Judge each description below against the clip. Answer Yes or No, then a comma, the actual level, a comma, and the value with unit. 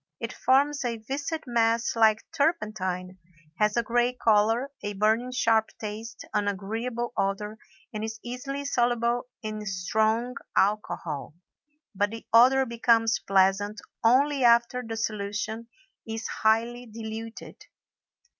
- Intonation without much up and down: Yes, narrow, 2.3 semitones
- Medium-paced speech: No, slow, 120 wpm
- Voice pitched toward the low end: No, high, 225 Hz